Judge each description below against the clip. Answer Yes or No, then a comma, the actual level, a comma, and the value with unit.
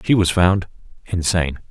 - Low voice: Yes, very low, 90 Hz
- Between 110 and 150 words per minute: Yes, average, 140 wpm